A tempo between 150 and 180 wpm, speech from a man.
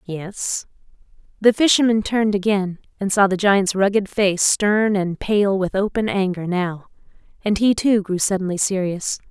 No: average, 155 wpm; female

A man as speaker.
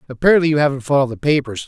Yes: male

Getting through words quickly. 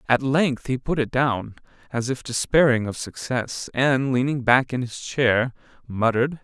No: average, 170 wpm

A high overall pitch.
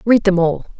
Yes: high, 195 Hz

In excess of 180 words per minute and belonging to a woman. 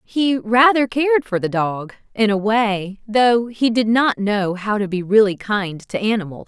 Yes: average, 195 wpm; female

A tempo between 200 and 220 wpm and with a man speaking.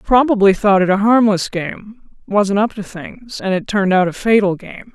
No: fast, 205 wpm; female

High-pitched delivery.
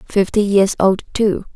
Yes: high, 200 Hz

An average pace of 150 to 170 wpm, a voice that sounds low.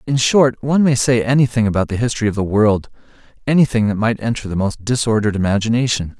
No: average, 185 wpm; low, 115 Hz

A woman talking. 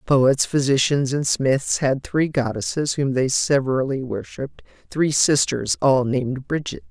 Yes: female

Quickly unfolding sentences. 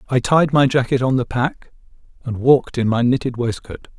No: average, 195 wpm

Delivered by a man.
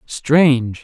Yes: male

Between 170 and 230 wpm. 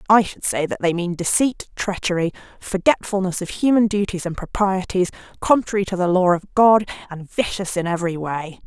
Yes: average, 175 wpm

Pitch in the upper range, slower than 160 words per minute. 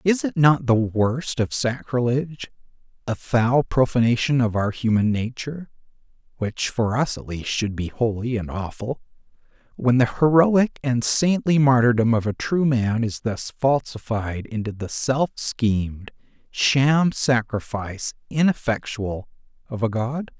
No: low, 120 Hz; average, 140 wpm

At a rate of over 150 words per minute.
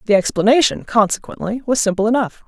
No: average, 145 wpm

